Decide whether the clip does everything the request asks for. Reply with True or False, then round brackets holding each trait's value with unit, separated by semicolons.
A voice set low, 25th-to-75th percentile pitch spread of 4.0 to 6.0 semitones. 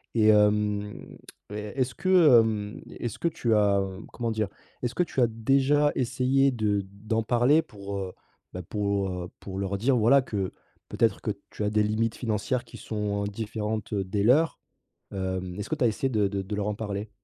False (105 Hz; 3.1 semitones)